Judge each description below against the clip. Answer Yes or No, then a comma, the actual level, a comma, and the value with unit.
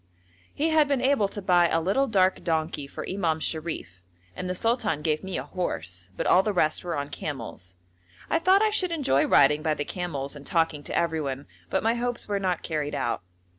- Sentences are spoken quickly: Yes, fast, 210 wpm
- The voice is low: No, medium, 170 Hz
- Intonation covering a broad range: Yes, wide, 6.0 semitones